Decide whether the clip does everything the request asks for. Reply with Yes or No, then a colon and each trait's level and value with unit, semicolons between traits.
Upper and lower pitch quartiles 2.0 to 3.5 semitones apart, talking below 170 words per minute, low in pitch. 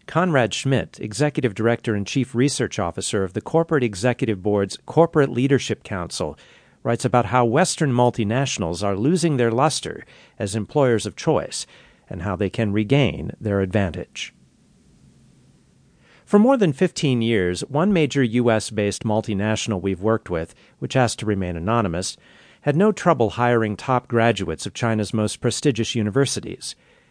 No: average, 4.7 semitones; average, 145 wpm; low, 115 Hz